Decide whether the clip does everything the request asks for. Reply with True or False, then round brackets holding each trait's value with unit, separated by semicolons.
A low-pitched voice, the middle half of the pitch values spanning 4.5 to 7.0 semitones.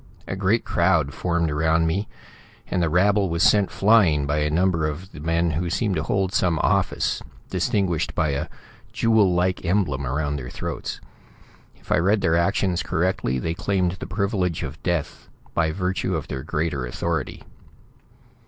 False (85 Hz; 3.6 semitones)